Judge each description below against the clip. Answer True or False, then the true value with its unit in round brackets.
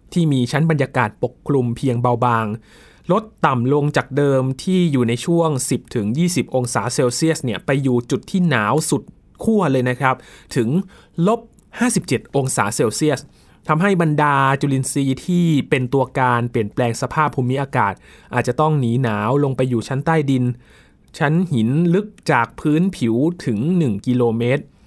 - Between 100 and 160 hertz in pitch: True (135 Hz)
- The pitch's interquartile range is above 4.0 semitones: True (4.4 semitones)